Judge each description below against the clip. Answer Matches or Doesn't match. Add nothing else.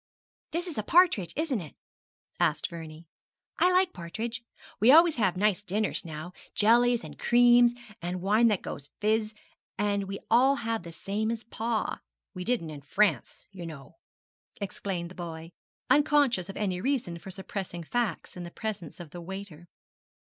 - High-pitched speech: Matches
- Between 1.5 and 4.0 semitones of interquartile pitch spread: Doesn't match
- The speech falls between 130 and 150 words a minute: Doesn't match